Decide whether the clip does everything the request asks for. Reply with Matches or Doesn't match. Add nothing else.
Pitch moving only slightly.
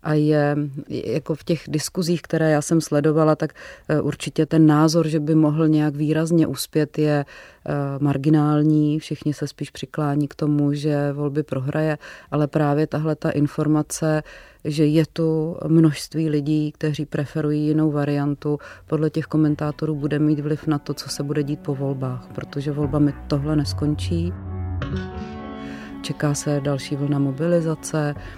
Matches